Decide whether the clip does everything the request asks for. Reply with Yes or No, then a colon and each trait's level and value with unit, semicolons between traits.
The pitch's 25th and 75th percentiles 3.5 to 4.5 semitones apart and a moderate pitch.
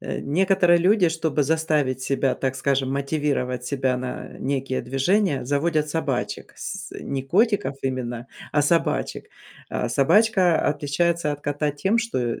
Yes: average, 4.2 semitones; medium, 145 Hz